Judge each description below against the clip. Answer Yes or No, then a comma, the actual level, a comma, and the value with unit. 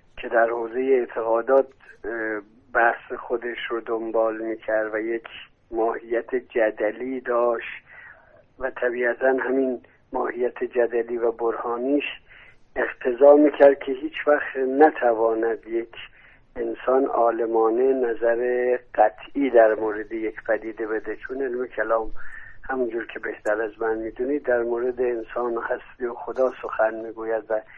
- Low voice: Yes, low, 115 Hz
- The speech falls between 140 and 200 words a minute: No, average, 120 wpm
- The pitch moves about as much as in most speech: No, narrow, 2.1 semitones